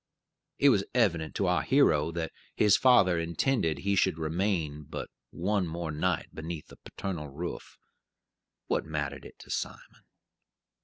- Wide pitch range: No, average, 3.9 semitones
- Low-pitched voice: Yes, very low, 85 Hz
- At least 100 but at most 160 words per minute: Yes, average, 145 wpm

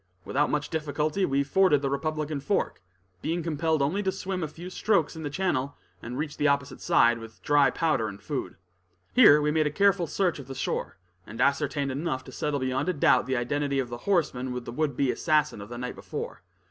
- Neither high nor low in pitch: Yes, medium, 145 Hz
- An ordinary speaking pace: No, fast, 215 wpm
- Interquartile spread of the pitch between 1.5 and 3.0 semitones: No, average, 3.4 semitones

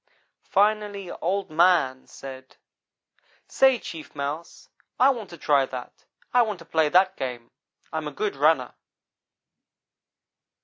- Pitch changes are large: Yes, wide, 6.2 semitones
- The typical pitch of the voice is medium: Yes, medium, 165 Hz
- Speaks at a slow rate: Yes, slow, 125 wpm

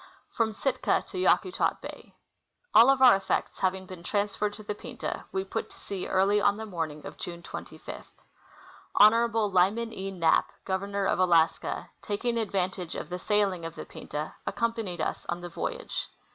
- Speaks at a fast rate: No, average, 170 wpm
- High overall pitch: Yes, high, 195 Hz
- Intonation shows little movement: No, average, 3.3 semitones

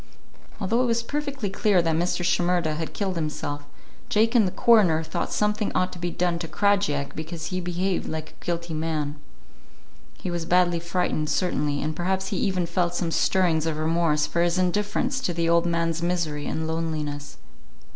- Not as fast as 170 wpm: No, average, 180 wpm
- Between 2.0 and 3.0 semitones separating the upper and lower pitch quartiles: Yes, average, 2.7 semitones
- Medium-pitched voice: Yes, medium, 175 Hz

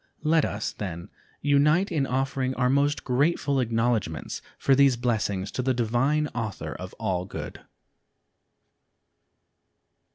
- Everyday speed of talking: No, slow, 120 wpm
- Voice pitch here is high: No, low, 125 Hz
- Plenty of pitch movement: No, average, 4.1 semitones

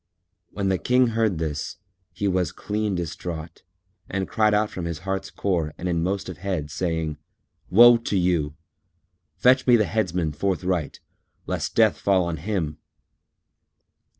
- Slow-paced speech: No, average, 150 wpm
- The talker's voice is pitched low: Yes, very low, 90 Hz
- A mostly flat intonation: No, average, 3.9 semitones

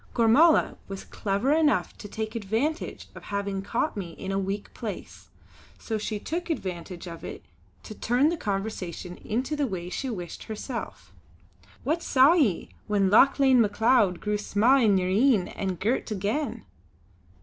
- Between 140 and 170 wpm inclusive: Yes, average, 155 wpm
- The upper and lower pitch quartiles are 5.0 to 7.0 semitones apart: Yes, average, 5.3 semitones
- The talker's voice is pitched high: Yes, high, 215 Hz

